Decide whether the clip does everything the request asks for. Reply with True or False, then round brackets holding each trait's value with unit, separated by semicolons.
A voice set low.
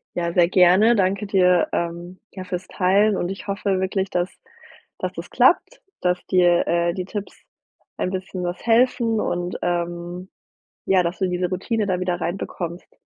False (185 Hz)